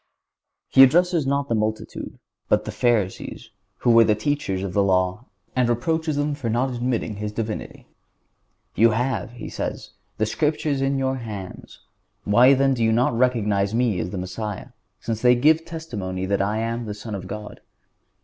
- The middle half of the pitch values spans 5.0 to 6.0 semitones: No, average, 4.3 semitones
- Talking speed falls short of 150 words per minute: No, average, 175 wpm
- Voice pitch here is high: No, low, 115 Hz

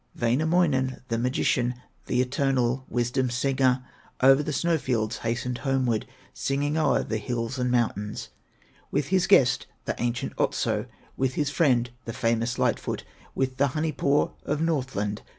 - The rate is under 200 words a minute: Yes, average, 150 wpm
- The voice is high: No, low, 130 Hz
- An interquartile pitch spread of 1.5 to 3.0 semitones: Yes, average, 2.7 semitones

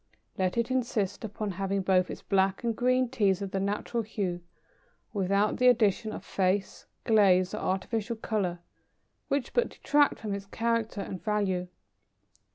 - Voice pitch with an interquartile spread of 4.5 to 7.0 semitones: No, average, 3.2 semitones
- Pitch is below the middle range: No, high, 205 Hz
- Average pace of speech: Yes, average, 155 wpm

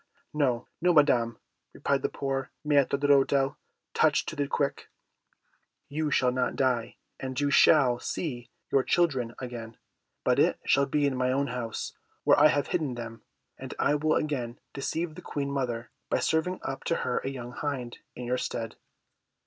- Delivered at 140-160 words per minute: No, average, 170 wpm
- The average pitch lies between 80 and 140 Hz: Yes, low, 135 Hz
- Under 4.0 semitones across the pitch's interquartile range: Yes, average, 2.8 semitones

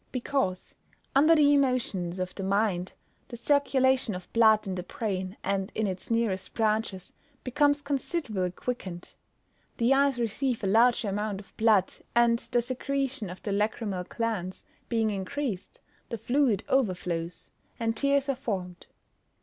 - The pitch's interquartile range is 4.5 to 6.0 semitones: Yes, wide, 5.4 semitones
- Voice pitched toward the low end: No, high, 225 Hz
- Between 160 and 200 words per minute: No, average, 145 wpm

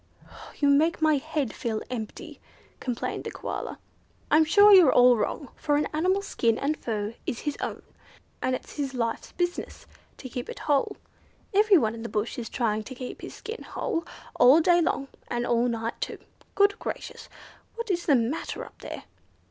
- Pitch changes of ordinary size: No, wide, 5.9 semitones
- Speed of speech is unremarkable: Yes, average, 180 wpm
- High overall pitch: Yes, very high, 275 Hz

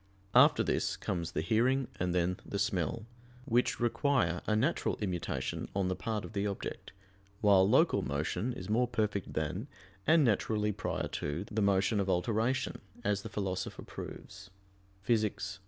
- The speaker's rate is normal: Yes, average, 155 wpm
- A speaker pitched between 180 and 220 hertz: No, low, 100 Hz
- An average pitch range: Yes, average, 3.4 semitones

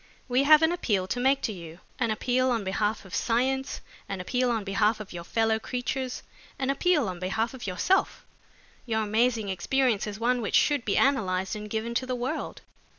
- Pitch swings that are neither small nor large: Yes, average, 4.0 semitones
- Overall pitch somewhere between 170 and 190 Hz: No, high, 230 Hz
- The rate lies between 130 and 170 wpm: No, average, 195 wpm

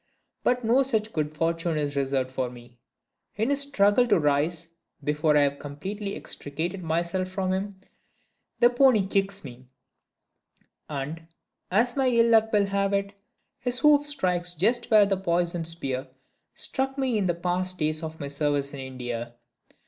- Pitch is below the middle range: No, medium, 180 Hz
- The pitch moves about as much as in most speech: No, wide, 6.4 semitones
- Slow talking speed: No, average, 160 wpm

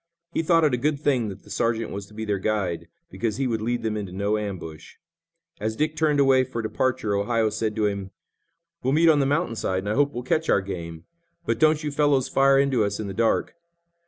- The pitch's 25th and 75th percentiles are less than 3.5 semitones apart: No, average, 5.2 semitones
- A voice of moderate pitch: No, low, 115 Hz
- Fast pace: Yes, fast, 235 wpm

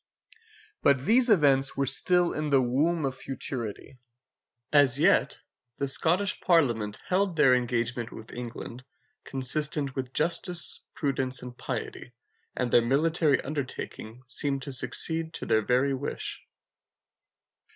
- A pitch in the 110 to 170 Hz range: Yes, low, 135 Hz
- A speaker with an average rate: No, slow, 125 wpm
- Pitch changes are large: No, average, 3.6 semitones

